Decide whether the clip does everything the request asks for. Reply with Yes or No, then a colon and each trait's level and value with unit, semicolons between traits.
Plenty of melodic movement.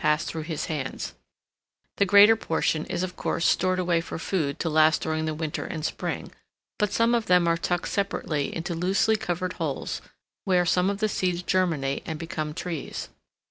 No: average, 2.9 semitones